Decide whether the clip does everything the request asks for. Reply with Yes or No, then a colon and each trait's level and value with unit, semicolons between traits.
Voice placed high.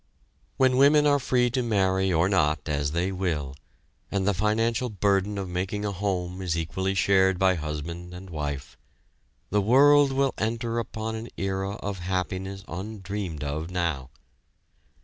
No: very low, 95 Hz